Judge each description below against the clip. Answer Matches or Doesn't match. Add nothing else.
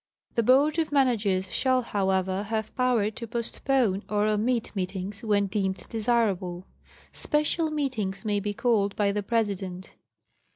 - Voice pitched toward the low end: Doesn't match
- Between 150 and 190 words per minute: Doesn't match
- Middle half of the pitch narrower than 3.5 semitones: Doesn't match